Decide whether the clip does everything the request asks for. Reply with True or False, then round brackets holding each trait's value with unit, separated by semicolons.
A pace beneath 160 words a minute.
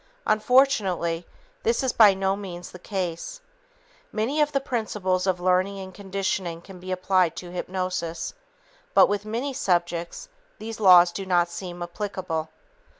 True (145 wpm)